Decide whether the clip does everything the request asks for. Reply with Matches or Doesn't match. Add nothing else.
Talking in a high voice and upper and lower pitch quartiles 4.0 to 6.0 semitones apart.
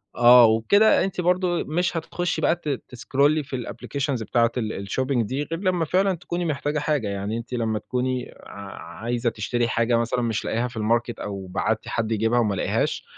Doesn't match